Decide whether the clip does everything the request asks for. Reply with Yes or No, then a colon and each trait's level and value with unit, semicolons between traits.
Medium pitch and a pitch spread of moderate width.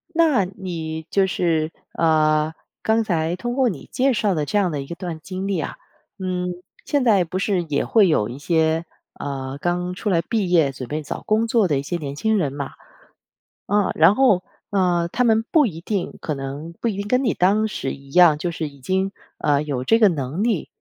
Yes: medium, 175 Hz; average, 5.0 semitones